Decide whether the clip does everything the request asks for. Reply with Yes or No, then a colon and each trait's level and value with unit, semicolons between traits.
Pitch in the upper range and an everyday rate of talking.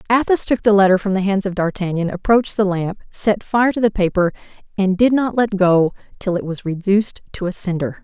No: high, 195 Hz; fast, 215 wpm